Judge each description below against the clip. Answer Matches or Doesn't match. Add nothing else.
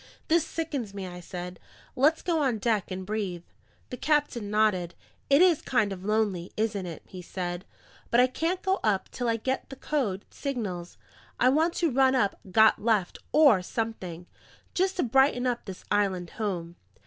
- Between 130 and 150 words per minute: Doesn't match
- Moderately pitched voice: Doesn't match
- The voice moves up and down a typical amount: Doesn't match